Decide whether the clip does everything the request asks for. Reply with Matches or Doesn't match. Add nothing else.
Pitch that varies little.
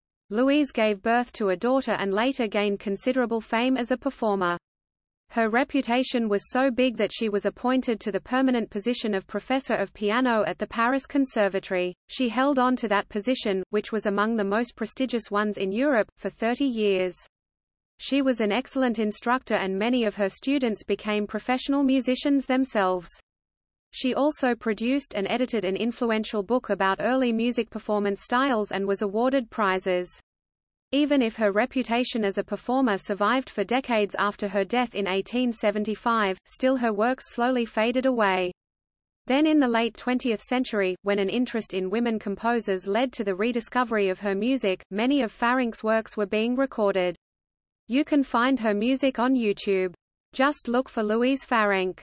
Doesn't match